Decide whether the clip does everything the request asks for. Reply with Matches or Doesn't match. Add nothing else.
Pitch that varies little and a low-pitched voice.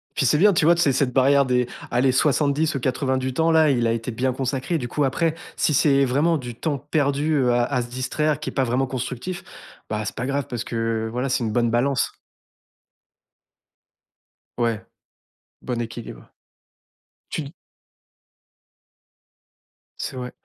Doesn't match